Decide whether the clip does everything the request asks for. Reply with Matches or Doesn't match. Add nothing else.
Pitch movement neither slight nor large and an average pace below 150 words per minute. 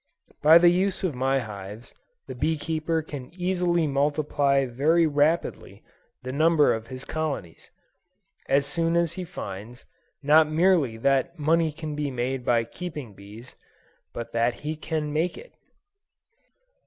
Matches